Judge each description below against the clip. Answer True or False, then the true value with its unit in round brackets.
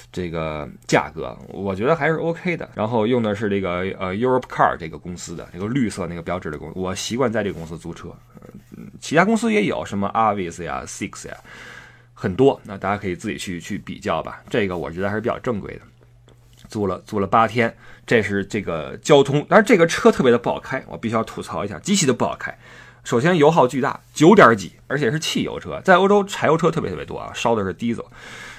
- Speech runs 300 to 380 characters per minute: True (365 characters per minute)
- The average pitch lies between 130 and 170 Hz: False (110 Hz)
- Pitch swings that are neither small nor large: False (6.8 semitones)